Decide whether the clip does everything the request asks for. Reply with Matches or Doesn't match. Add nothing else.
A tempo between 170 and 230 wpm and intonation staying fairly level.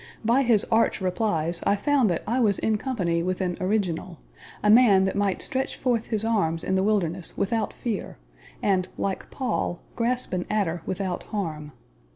Doesn't match